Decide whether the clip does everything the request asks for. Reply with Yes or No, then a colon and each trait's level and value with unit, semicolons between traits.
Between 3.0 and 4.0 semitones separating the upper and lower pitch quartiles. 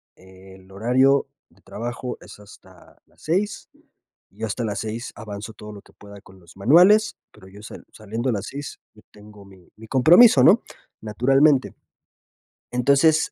No: average, 5.2 semitones